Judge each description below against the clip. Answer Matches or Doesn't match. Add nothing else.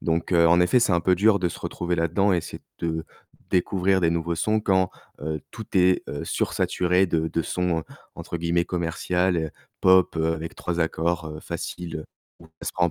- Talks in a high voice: Doesn't match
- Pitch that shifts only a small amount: Matches